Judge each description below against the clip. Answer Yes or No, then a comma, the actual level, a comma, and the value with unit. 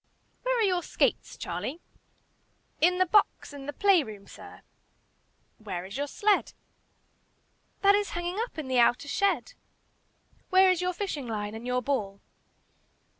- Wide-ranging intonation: Yes, wide, 8.2 semitones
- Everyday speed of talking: Yes, average, 150 wpm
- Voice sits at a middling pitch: No, very high, 315 Hz